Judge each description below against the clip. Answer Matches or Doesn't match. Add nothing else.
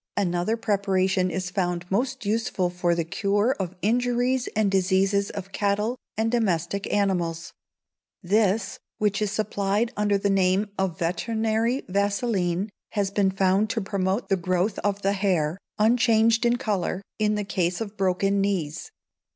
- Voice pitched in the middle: Doesn't match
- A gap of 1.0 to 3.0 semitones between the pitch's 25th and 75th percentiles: Matches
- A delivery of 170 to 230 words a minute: Doesn't match